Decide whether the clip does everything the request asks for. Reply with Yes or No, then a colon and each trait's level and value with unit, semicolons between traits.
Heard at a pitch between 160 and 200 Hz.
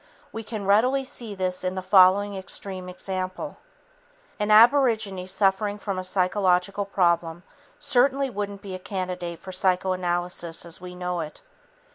Yes: high, 190 Hz